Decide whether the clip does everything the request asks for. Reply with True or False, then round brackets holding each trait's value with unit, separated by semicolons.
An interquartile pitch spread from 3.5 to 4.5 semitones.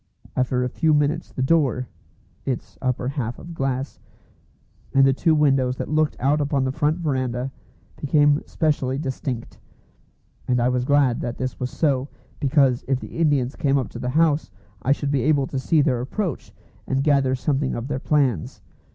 False (2.5 semitones)